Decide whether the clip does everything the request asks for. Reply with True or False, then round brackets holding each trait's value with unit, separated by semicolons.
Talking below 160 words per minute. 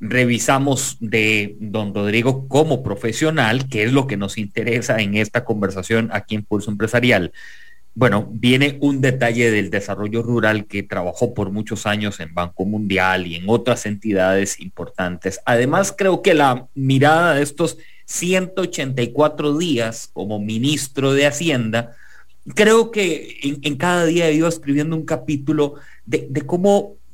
True (145 wpm)